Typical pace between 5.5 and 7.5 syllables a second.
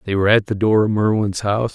Yes: 6.8 syllables/s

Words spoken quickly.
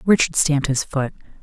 No: average, 170 wpm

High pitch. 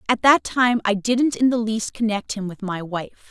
Yes: high, 220 Hz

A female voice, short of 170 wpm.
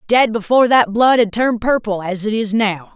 No: female; fast, 205 wpm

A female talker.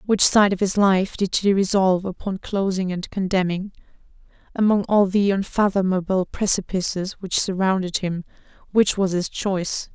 Yes: female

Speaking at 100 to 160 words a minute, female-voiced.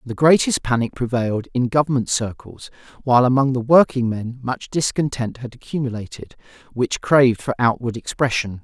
No: average, 140 wpm; male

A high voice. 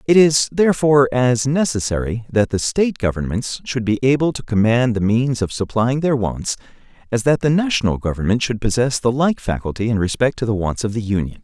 No: low, 120 Hz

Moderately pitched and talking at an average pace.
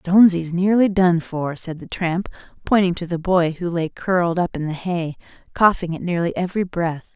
Yes: medium, 175 Hz; average, 195 wpm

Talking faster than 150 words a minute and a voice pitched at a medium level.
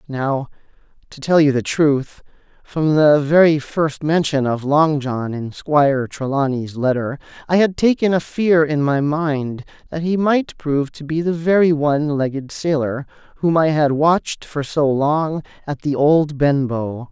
Yes: average, 170 wpm; medium, 150 Hz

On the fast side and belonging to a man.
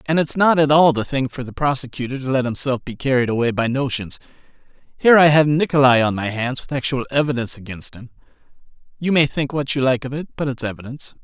Yes: fast, 215 wpm; male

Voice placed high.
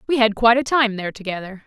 Yes: high, 225 Hz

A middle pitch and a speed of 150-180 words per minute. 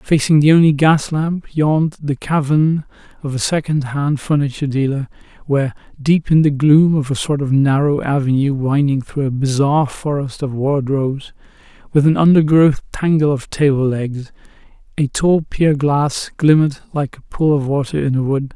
Yes: medium, 145 Hz; average, 165 wpm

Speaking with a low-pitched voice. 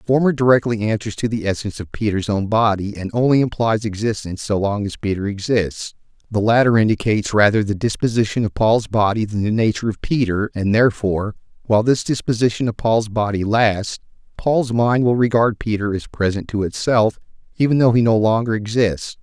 Yes: low, 110 Hz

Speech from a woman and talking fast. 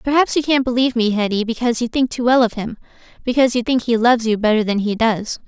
Yes: female; fast, 240 wpm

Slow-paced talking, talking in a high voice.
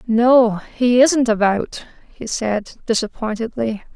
Yes: slow, 105 wpm; high, 230 Hz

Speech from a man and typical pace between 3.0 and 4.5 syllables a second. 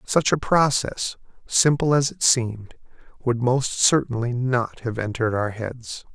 Yes: male; 4.2 syllables/s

